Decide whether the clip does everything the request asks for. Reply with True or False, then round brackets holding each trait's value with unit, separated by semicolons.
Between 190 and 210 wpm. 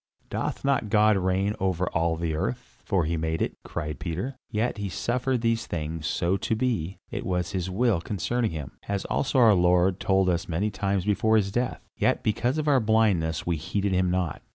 True (200 wpm)